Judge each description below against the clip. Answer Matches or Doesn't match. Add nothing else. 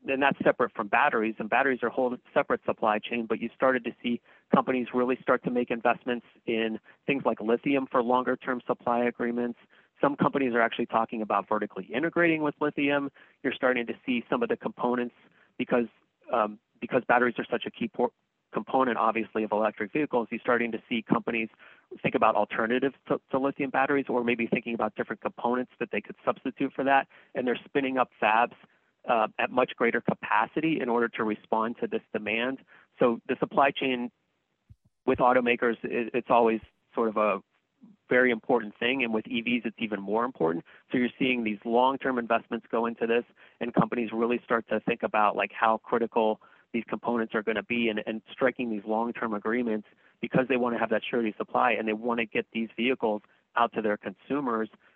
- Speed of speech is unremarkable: Matches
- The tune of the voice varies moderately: Doesn't match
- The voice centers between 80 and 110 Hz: Doesn't match